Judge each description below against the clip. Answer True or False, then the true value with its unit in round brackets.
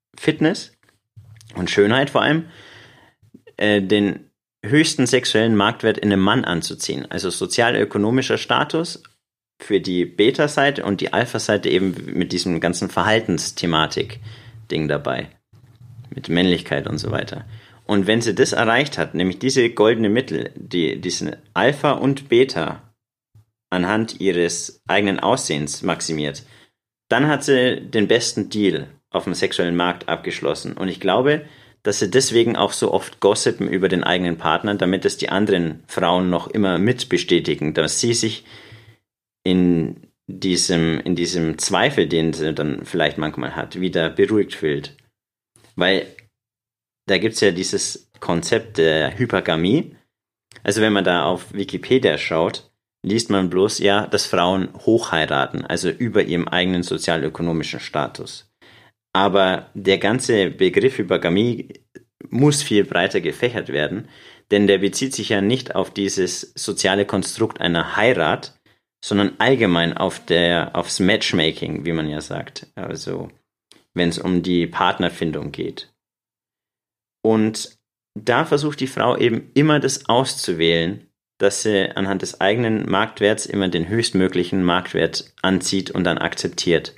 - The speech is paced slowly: False (135 wpm)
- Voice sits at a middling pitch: False (100 Hz)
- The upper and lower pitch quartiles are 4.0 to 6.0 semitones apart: True (4.6 semitones)